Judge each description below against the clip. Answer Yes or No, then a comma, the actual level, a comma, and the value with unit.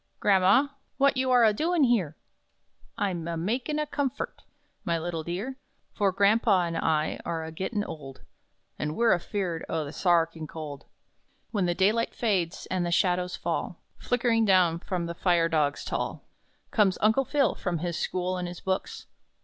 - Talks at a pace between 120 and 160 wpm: No, average, 170 wpm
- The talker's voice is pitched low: No, medium, 185 Hz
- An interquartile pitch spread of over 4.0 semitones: Yes, average, 5.2 semitones